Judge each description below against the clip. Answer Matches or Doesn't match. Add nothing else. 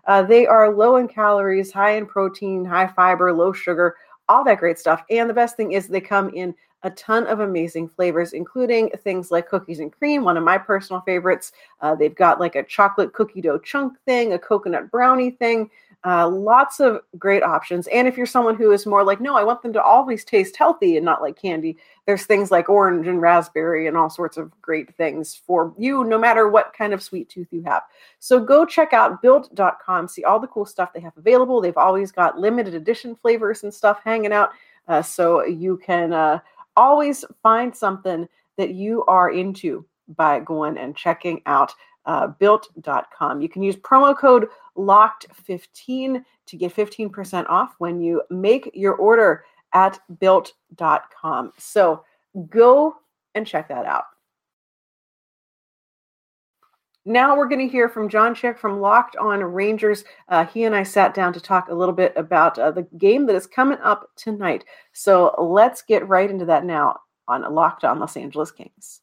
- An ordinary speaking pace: Matches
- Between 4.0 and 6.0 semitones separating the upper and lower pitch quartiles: Matches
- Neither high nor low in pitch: Doesn't match